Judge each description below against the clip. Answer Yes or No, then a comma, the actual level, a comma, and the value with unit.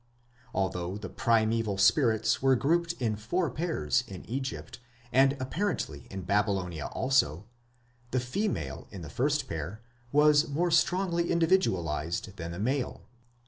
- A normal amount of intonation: No, wide, 7.8 semitones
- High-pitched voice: No, low, 120 Hz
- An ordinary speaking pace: No, slow, 130 wpm